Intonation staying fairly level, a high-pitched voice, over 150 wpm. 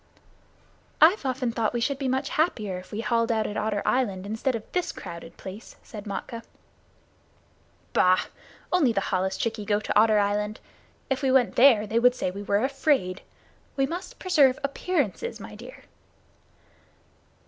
No: average, 4.7 semitones; high, 230 Hz; average, 160 wpm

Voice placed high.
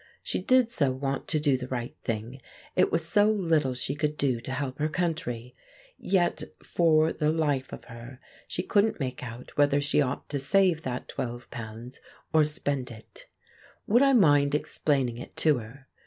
No: medium, 140 Hz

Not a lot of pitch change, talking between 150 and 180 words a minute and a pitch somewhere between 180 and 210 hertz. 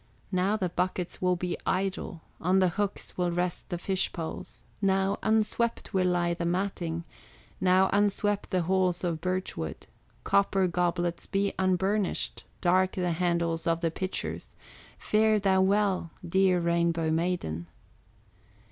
No: narrow, 2.0 semitones; average, 140 wpm; medium, 185 Hz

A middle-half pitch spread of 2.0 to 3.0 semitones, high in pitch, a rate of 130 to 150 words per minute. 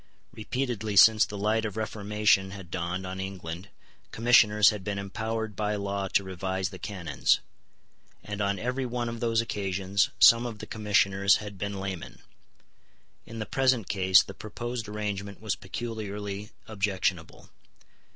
No: narrow, 2.4 semitones; low, 105 Hz; average, 145 wpm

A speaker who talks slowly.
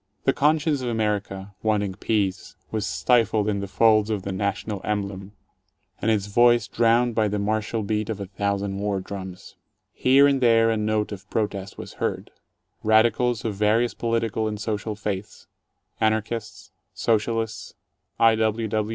No: average, 155 wpm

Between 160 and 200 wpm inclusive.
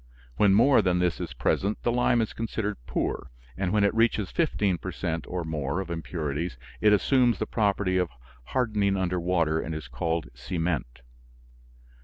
Yes: average, 170 wpm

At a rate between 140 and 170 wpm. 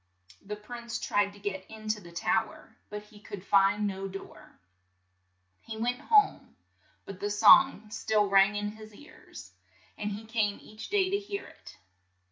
No: average, 180 wpm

